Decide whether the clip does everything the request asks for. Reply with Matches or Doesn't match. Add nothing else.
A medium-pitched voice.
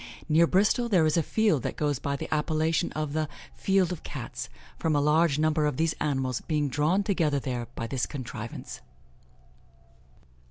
Matches